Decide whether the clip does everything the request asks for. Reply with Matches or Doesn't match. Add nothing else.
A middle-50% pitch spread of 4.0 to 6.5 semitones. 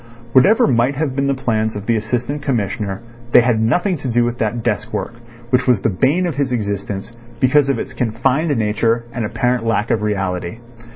Doesn't match